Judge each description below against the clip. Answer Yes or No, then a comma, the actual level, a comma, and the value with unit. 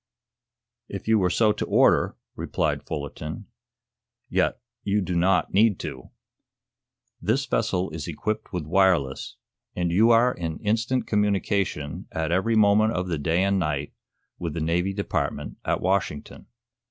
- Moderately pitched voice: No, very low, 95 Hz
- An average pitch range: Yes, average, 4.1 semitones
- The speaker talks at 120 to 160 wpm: Yes, average, 140 wpm